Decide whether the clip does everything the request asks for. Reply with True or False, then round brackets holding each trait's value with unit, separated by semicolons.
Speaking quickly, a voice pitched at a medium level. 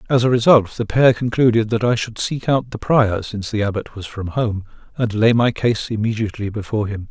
False (220 wpm; 110 Hz)